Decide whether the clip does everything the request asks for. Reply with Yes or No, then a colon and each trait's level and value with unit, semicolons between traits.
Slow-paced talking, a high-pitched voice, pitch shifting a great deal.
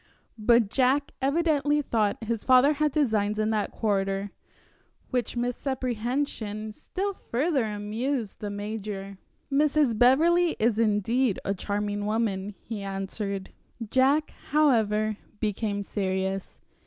No: slow, 110 wpm; high, 220 Hz; average, 4.5 semitones